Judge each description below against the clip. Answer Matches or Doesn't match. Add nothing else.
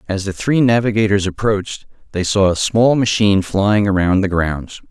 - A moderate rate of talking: Matches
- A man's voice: Matches